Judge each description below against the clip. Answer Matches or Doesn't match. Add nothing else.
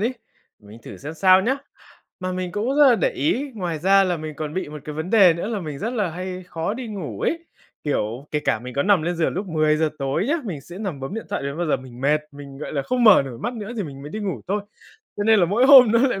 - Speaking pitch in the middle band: Matches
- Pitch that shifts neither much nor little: Doesn't match